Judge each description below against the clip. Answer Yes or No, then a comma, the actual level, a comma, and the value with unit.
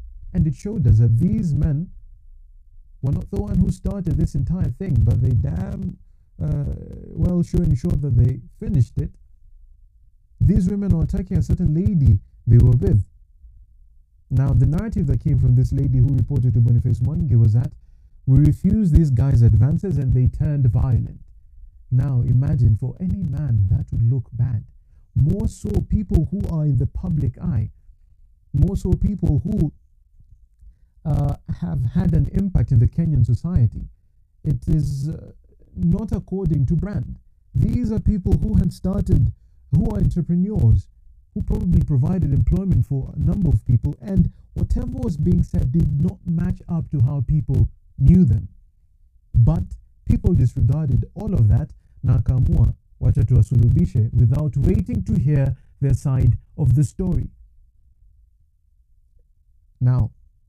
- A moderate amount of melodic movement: No, wide, 8.1 semitones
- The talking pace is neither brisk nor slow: Yes, average, 145 wpm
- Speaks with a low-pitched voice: Yes, low, 120 Hz